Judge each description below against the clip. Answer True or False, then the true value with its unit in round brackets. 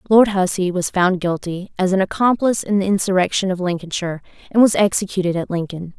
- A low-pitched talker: False (185 Hz)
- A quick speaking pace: False (180 wpm)